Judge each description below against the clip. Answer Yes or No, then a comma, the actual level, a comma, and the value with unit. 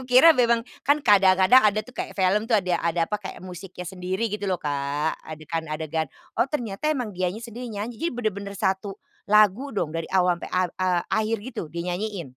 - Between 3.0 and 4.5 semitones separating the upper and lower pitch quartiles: Yes, average, 4.1 semitones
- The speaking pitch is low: No, high, 195 Hz